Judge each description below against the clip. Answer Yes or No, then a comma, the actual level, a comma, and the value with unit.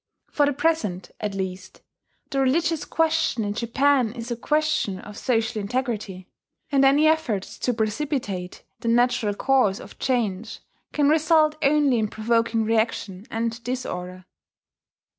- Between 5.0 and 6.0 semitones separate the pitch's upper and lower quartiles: Yes, average, 5.3 semitones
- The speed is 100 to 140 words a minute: Yes, slow, 135 wpm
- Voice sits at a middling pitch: No, high, 235 Hz